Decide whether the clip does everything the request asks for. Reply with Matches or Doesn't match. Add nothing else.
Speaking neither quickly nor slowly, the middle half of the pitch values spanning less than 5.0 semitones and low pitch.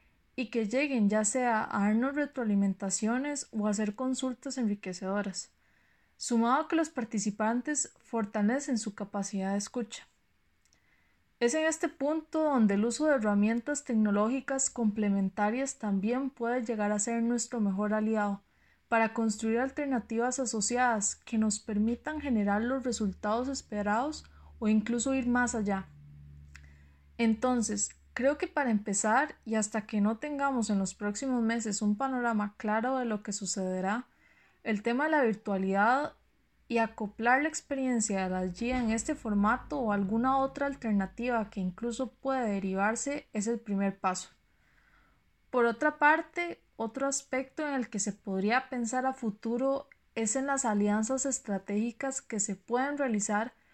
Doesn't match